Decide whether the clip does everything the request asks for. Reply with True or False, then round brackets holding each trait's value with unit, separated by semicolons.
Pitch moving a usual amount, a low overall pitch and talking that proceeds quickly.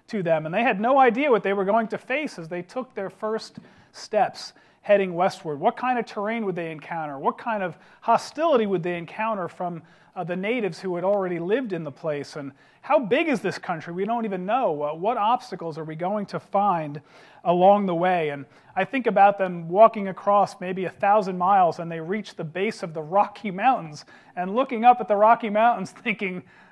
False (4.3 semitones; 195 Hz; 215 wpm)